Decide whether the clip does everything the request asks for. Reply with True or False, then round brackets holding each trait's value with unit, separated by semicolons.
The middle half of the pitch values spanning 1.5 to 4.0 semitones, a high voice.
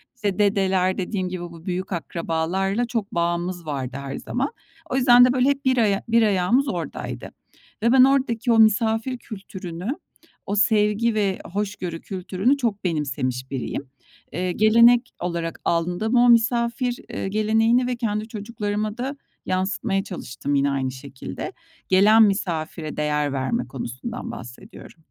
False (5.3 semitones; 200 Hz)